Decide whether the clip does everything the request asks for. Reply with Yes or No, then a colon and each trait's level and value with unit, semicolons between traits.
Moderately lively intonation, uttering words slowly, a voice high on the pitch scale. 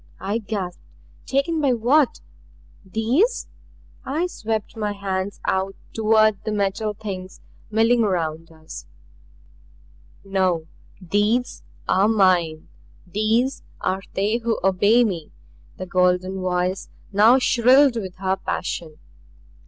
Yes: average, 3.4 semitones; slow, 110 wpm; high, 205 Hz